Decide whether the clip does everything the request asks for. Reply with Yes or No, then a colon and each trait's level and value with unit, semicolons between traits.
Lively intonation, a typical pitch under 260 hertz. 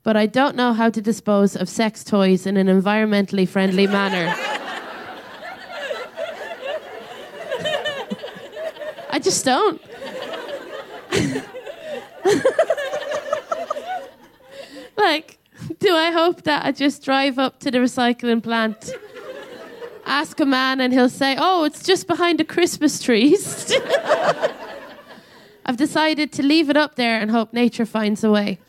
No: wide, 6.3 semitones; very high, 275 Hz